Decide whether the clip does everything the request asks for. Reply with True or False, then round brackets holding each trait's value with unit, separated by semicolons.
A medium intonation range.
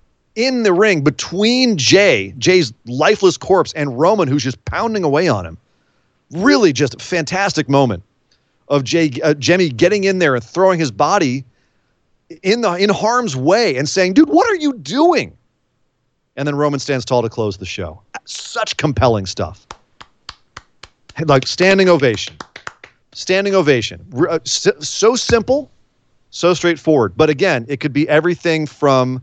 False (6.6 semitones)